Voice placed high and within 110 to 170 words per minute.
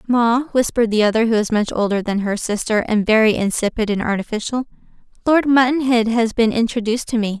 No: high, 225 Hz; average, 185 wpm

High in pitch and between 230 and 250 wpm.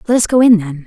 No: high, 205 Hz; fast, 350 wpm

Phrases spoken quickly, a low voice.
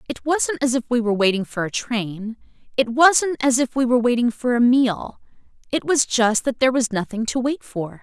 No: fast, 215 wpm; high, 240 Hz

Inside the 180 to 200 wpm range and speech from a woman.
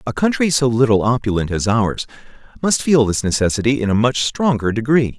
No: average, 185 wpm; male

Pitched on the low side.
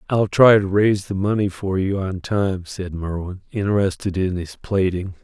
Yes: very low, 95 Hz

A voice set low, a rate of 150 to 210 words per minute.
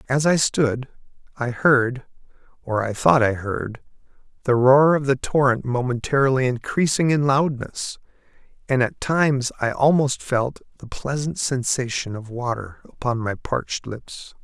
No: low, 130 Hz; average, 140 wpm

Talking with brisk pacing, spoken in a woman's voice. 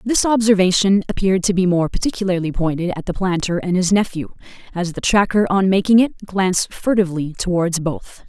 No: average, 175 wpm; female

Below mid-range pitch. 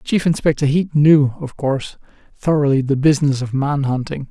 No: medium, 145 Hz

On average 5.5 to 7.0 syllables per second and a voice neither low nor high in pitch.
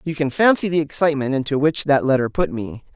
Yes: 6.1 syllables/s; medium, 145 Hz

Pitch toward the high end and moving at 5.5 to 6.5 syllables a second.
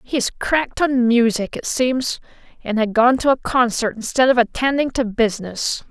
No: high, 240 Hz; 4.7 syllables/s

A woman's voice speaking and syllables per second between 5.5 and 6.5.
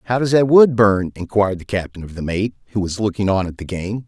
No: male; 6.0 syllables/s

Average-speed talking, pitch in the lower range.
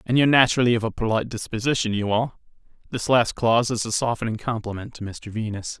Yes: average, 195 wpm; low, 115 Hz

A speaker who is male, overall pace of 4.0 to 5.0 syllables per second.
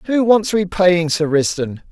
Yes: male; 4.1 syllables/s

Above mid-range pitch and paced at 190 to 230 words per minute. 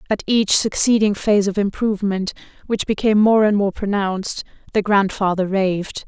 No: high, 205 Hz; average, 150 wpm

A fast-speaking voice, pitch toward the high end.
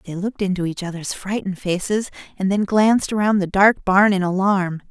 No: average, 195 wpm; high, 195 Hz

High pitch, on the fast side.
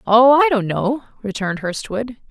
No: high, 230 Hz; average, 155 wpm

